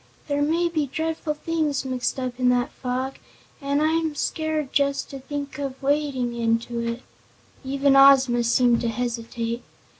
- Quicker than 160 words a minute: No, average, 150 wpm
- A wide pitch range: No, average, 3.2 semitones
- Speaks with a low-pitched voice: No, very high, 270 Hz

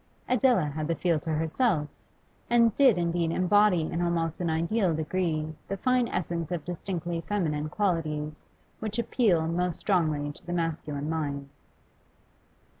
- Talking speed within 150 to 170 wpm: No, average, 140 wpm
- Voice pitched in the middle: Yes, medium, 170 Hz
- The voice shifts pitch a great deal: No, average, 3.7 semitones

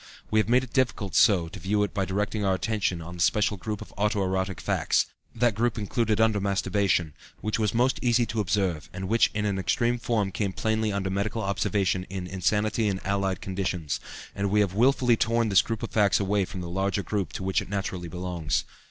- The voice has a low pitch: Yes, low, 100 Hz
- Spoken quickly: Yes, fast, 215 wpm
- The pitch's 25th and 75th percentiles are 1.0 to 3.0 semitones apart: Yes, narrow, 2.5 semitones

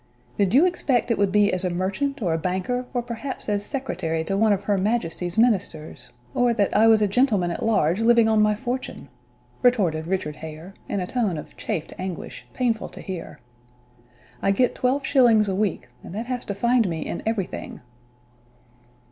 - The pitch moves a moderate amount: Yes, average, 4.7 semitones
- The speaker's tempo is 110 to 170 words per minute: No, average, 190 wpm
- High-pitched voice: Yes, high, 210 Hz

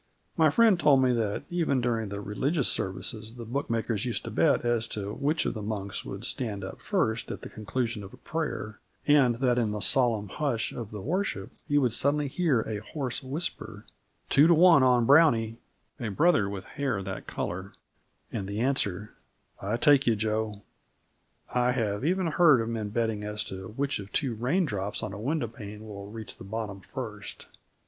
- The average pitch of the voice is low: Yes, low, 115 Hz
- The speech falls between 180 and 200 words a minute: Yes, average, 190 wpm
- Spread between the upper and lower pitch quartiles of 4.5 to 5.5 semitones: Yes, average, 4.9 semitones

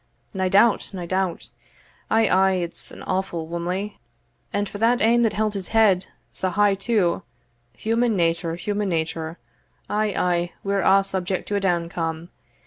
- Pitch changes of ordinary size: Yes, average, 3.1 semitones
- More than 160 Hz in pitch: Yes, high, 190 Hz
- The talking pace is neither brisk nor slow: Yes, average, 150 wpm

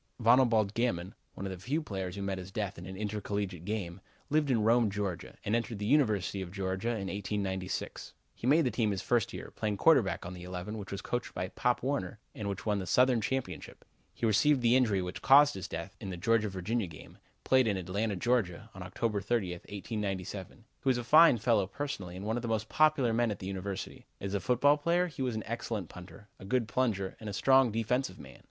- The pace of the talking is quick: Yes, fast, 220 wpm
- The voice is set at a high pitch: No, low, 105 Hz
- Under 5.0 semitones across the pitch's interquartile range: Yes, average, 4.1 semitones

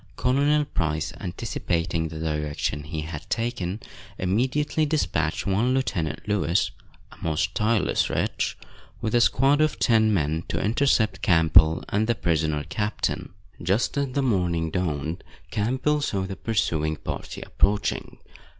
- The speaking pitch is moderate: No, very low, 95 Hz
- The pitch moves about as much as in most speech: No, wide, 6.7 semitones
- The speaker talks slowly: Yes, slow, 130 wpm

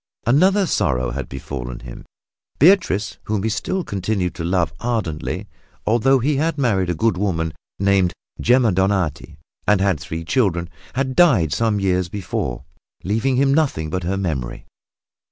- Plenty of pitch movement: Yes, wide, 6.8 semitones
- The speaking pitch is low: Yes, low, 100 Hz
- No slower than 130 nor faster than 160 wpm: Yes, average, 150 wpm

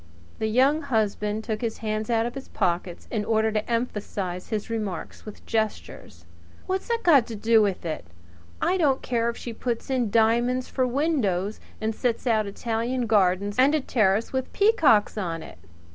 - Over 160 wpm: Yes, average, 175 wpm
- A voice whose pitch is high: Yes, high, 225 Hz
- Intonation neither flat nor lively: Yes, average, 3.2 semitones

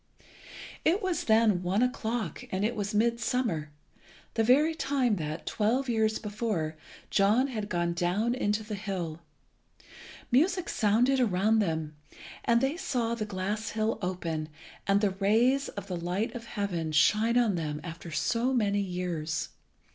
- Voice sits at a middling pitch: No, high, 210 Hz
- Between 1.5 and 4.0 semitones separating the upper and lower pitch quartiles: No, average, 4.7 semitones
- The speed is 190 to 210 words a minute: No, average, 145 wpm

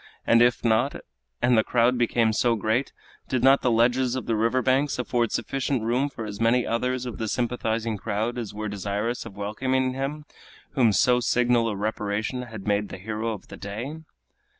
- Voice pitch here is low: Yes, low, 115 Hz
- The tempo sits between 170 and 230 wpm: Yes, average, 190 wpm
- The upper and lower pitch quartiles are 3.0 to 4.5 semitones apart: No, narrow, 2.5 semitones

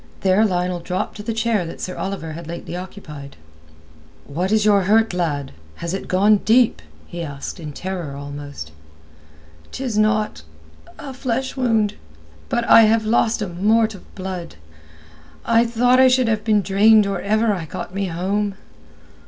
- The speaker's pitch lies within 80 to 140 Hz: No, high, 200 Hz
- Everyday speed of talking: Yes, average, 160 wpm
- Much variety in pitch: No, average, 4.5 semitones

